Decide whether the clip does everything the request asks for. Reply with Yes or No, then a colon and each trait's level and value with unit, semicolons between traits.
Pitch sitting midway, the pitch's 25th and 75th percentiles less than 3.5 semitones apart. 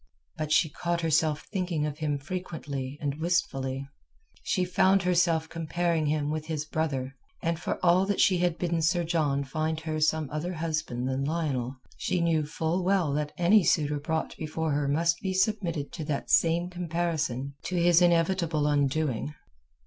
Yes: medium, 160 Hz; average, 2.7 semitones